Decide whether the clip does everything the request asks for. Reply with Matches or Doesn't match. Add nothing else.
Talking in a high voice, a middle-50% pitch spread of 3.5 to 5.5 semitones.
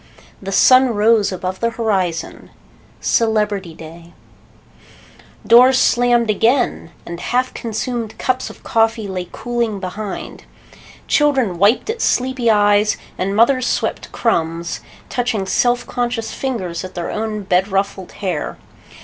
Matches